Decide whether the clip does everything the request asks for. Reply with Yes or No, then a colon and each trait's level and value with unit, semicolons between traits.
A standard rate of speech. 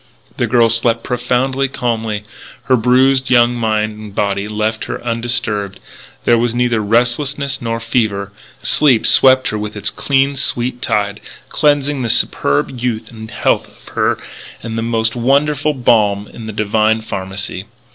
Yes: average, 150 wpm